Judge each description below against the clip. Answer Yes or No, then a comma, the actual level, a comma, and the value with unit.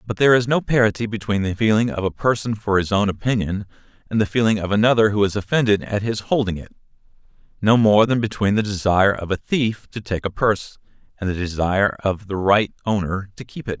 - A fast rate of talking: Yes, fast, 215 wpm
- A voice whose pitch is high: No, low, 105 Hz